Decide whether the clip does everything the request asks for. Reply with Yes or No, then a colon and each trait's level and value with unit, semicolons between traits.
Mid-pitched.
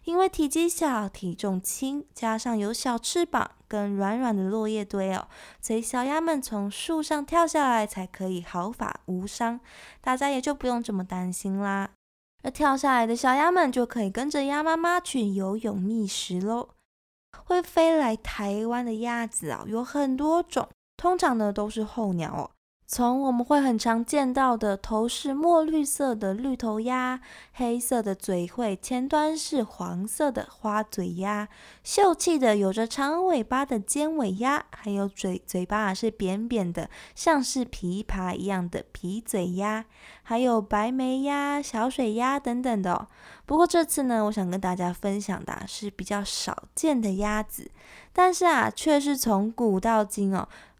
No: high, 230 Hz